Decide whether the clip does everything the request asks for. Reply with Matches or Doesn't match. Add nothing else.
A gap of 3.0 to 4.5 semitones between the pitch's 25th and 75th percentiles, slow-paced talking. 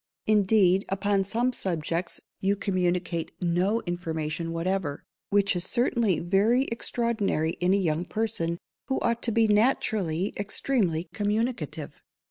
Matches